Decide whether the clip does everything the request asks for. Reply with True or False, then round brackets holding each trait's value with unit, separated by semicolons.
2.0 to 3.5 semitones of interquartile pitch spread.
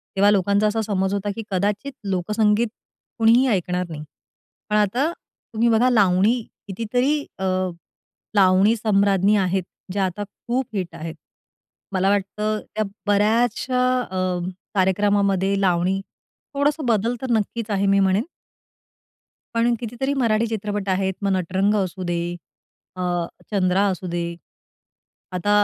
True (2.9 semitones)